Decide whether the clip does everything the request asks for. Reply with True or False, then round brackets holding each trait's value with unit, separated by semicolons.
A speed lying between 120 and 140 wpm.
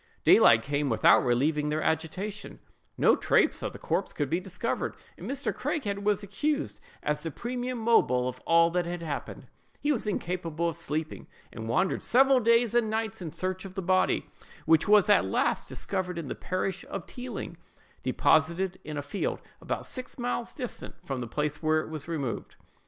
False (180 wpm)